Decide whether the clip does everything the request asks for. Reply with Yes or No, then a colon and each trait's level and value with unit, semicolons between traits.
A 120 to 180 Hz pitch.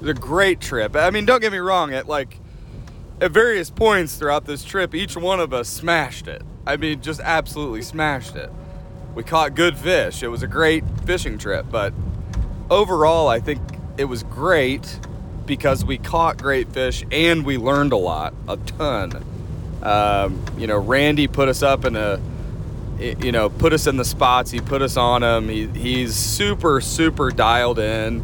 Yes: low, 135 Hz